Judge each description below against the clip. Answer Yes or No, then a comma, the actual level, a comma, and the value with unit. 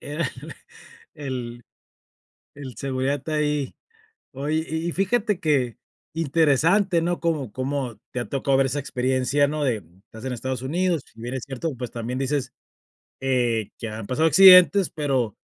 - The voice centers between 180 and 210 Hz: No, low, 135 Hz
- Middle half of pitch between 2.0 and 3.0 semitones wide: No, average, 4.1 semitones